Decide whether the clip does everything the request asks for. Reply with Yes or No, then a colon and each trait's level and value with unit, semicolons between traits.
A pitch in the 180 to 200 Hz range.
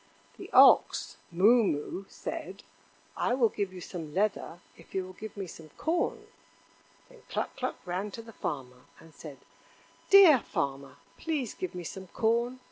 Yes: high, 190 Hz